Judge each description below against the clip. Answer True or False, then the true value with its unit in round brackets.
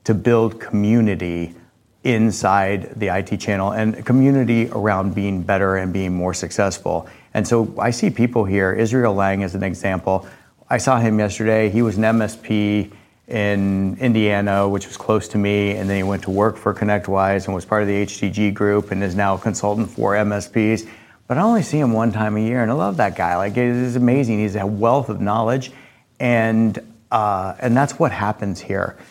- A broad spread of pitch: False (2.5 semitones)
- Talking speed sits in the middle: True (190 wpm)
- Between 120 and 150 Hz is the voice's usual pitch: False (105 Hz)